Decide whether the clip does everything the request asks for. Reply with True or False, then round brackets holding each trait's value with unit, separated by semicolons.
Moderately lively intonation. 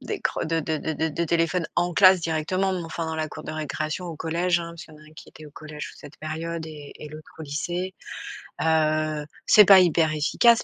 False (2.0 semitones)